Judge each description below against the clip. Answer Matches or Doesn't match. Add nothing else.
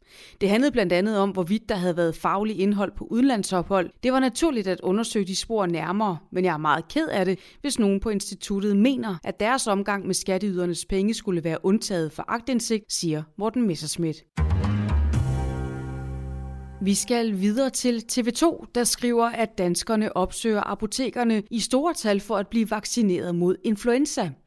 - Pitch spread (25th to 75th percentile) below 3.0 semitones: Doesn't match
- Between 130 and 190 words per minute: Matches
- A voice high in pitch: Matches